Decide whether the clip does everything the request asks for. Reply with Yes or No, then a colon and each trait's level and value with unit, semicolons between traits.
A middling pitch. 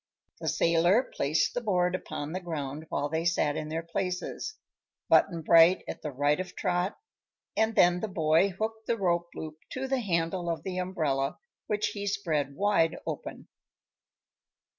Yes: medium, 175 Hz